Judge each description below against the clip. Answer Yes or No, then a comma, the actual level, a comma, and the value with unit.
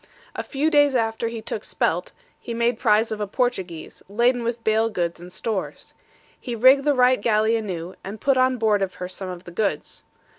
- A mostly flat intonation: No, average, 3.7 semitones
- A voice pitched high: Yes, high, 225 Hz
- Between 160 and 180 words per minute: No, average, 200 wpm